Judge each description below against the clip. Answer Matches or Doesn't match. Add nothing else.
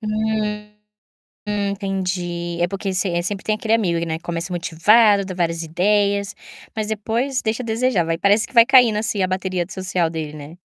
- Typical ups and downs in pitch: Matches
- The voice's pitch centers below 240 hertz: Matches